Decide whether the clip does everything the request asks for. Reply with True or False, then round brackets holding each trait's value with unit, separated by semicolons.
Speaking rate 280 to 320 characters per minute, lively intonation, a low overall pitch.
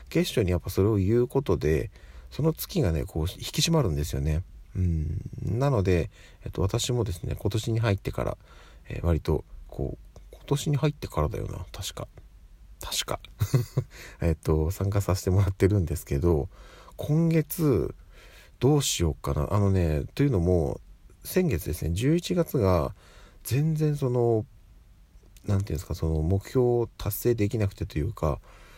True (285 characters per minute; 6.4 semitones; 100 Hz)